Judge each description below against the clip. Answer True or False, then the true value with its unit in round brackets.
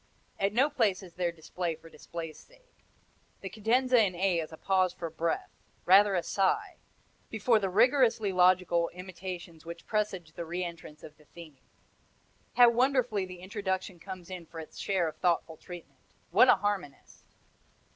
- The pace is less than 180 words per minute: True (165 wpm)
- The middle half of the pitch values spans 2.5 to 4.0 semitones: True (3.5 semitones)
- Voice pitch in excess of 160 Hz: True (185 Hz)